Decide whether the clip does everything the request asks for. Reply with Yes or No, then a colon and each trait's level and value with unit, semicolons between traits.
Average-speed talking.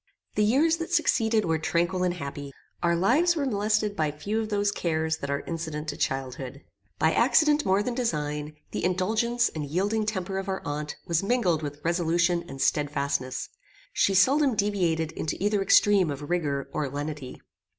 Yes: average, 170 wpm